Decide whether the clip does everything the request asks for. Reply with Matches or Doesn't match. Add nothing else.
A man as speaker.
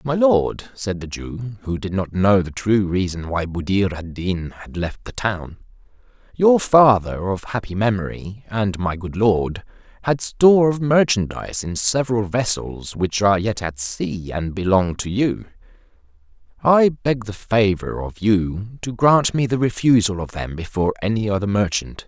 Matches